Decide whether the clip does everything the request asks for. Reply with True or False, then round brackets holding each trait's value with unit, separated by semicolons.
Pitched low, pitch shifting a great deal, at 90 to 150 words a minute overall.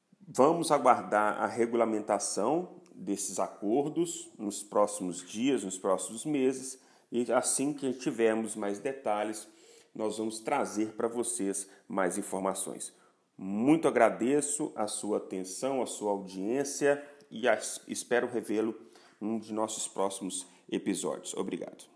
False (110 Hz; 4.7 semitones; 120 wpm)